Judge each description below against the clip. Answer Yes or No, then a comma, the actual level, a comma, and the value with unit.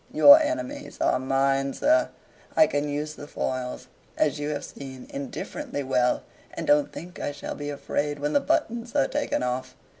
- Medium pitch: Yes, medium, 145 Hz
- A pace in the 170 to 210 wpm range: Yes, average, 180 wpm